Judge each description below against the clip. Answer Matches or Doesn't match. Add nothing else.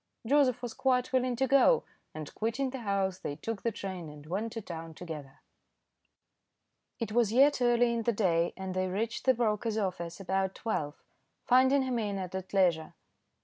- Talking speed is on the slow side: Doesn't match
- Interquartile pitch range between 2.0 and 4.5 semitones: Doesn't match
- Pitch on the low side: Doesn't match